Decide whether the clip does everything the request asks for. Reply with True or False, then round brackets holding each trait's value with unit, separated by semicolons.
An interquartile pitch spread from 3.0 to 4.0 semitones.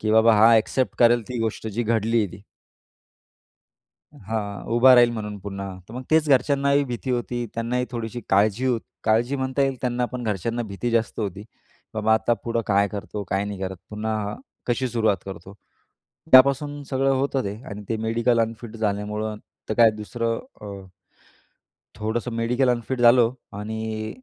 False (2.6 semitones)